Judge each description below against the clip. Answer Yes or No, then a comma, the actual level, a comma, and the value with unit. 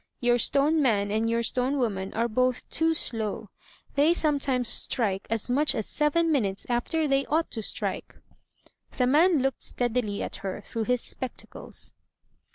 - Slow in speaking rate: No, average, 160 wpm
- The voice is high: Yes, very high, 250 Hz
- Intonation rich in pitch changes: No, average, 4.5 semitones